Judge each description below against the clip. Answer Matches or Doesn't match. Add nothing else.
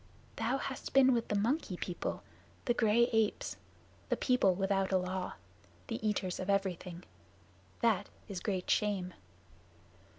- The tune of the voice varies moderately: Matches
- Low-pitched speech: Doesn't match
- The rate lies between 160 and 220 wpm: Doesn't match